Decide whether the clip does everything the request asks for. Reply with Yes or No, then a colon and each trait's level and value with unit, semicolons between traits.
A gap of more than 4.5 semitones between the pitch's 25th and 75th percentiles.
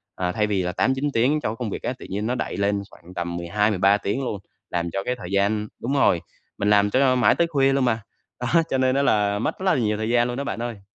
No: average, 4.2 semitones